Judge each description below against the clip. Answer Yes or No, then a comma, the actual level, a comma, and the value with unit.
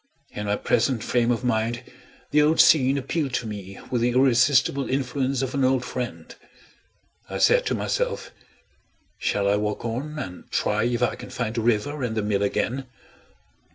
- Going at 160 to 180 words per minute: Yes, average, 175 wpm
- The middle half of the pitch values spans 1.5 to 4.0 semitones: Yes, average, 3.6 semitones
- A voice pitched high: No, low, 125 Hz